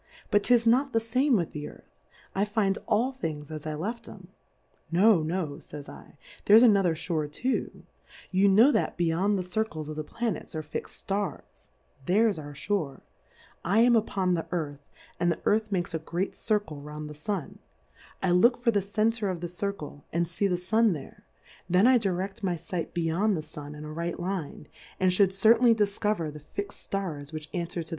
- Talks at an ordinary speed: Yes, average, 195 wpm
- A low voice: No, medium, 185 Hz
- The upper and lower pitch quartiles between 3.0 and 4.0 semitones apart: No, average, 4.8 semitones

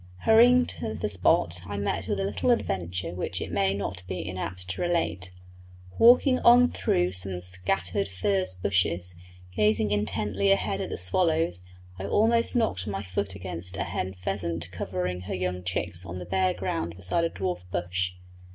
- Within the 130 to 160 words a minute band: No, average, 170 wpm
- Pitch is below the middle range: Yes, very low, 95 Hz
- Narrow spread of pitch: Yes, narrow, 2.2 semitones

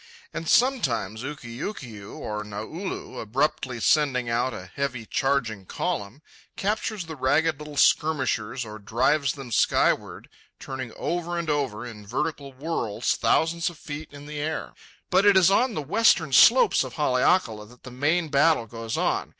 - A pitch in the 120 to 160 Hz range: Yes, medium, 140 Hz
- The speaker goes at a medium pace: Yes, average, 150 wpm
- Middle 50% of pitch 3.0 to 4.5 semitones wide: No, wide, 5.6 semitones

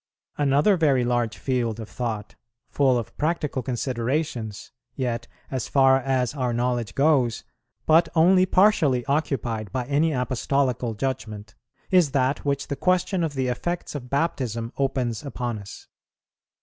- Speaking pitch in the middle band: No, low, 130 Hz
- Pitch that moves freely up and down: No, average, 3.4 semitones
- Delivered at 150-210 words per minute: No, slow, 135 wpm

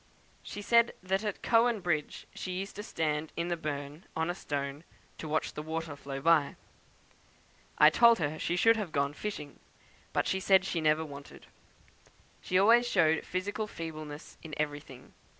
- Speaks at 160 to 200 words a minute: Yes, average, 165 wpm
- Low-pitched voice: No, medium, 165 Hz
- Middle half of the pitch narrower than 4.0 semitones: No, average, 4.4 semitones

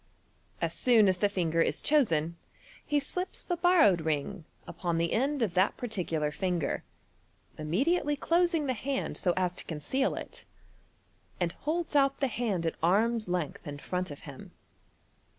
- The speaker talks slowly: No, average, 160 wpm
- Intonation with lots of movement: Yes, wide, 8.6 semitones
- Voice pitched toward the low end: No, high, 195 Hz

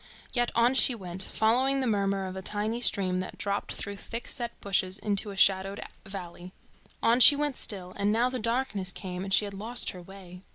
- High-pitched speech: Yes, high, 200 Hz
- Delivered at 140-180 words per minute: No, fast, 205 wpm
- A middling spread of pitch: Yes, average, 3.7 semitones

